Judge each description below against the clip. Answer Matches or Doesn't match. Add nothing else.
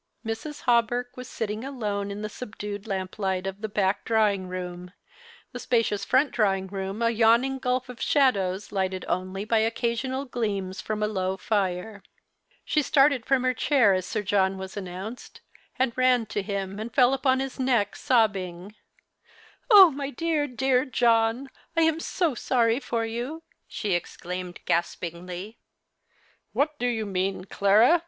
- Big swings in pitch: Doesn't match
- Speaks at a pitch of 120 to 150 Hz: Doesn't match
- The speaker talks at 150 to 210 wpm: Matches